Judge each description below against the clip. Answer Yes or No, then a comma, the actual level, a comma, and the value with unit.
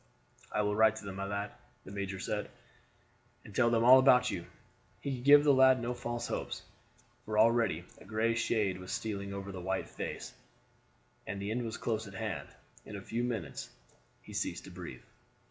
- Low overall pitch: Yes, low, 110 Hz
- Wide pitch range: No, average, 3.2 semitones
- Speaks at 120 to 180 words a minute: No, average, 195 wpm